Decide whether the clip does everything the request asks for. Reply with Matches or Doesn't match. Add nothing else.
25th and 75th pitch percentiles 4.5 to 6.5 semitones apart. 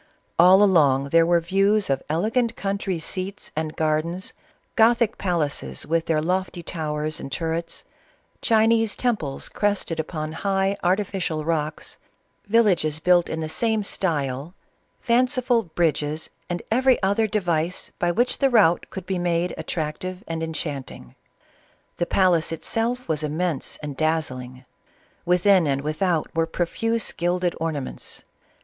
Doesn't match